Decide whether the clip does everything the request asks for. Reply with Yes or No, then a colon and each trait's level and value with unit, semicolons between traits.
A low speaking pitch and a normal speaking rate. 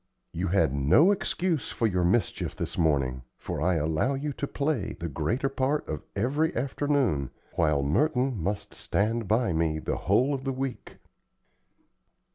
Yes: low, 110 Hz; average, 155 wpm